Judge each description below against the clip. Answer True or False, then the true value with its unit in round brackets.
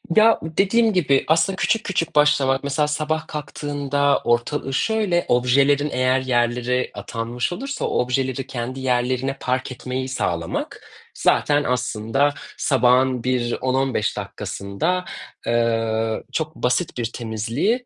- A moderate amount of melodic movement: True (3.6 semitones)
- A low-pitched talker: True (130 Hz)